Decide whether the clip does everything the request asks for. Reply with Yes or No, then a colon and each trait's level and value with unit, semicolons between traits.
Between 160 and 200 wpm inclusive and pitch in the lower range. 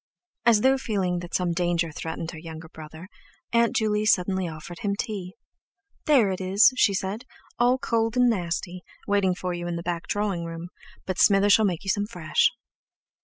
No: average, 180 wpm; medium, 185 Hz